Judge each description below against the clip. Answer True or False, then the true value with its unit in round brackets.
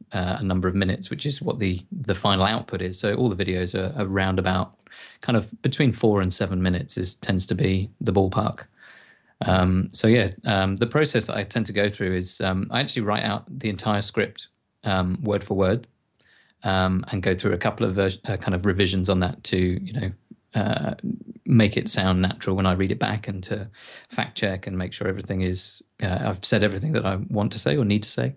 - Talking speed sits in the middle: False (225 wpm)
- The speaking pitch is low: True (95 Hz)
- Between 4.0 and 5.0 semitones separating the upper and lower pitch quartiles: False (2.9 semitones)